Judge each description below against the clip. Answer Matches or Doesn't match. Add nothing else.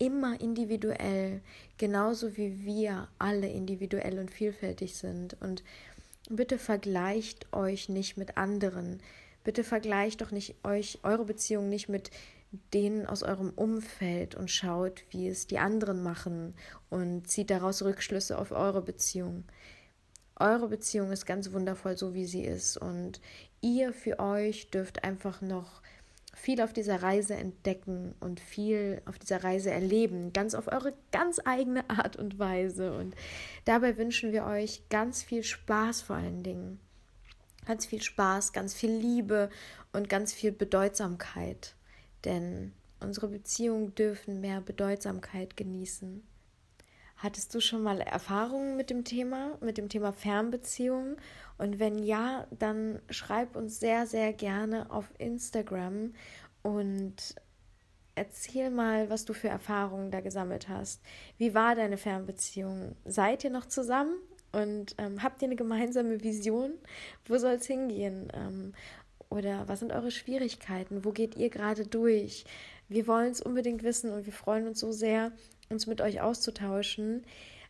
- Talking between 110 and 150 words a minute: Matches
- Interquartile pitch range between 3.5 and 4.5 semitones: Doesn't match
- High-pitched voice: Matches